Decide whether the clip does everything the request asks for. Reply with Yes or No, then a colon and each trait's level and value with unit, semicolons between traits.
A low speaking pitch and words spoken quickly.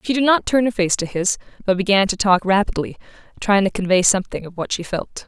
No: high, 195 Hz; fast, 240 wpm